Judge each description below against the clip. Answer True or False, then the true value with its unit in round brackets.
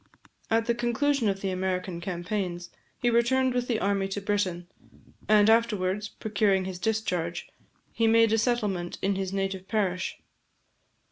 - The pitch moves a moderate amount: True (3.4 semitones)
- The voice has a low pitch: False (205 Hz)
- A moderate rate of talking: True (145 wpm)